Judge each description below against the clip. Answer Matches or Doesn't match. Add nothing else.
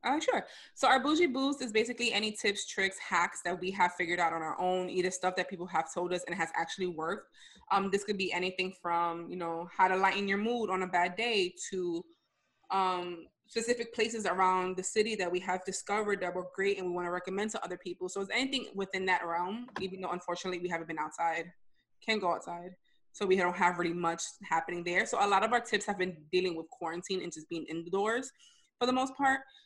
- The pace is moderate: Doesn't match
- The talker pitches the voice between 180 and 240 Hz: Matches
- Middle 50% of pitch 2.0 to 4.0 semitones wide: Matches